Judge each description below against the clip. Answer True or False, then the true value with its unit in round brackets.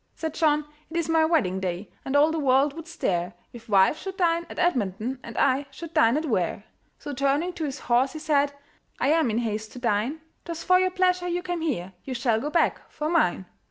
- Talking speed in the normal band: False (225 wpm)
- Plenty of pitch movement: True (6.1 semitones)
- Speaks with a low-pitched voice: False (285 Hz)